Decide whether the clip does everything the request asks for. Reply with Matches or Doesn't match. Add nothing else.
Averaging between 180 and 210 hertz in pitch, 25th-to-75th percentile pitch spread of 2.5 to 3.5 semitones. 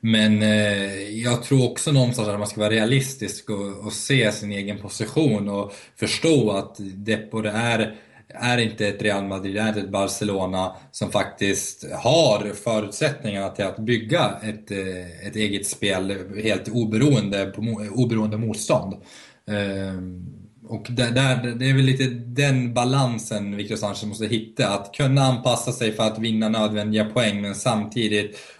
Doesn't match